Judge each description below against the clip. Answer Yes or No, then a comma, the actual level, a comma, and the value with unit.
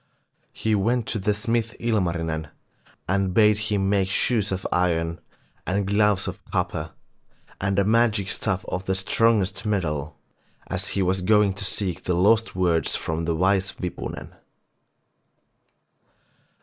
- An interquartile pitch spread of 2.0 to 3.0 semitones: Yes, average, 2.7 semitones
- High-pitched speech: No, very low, 95 Hz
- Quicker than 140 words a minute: No, slow, 135 wpm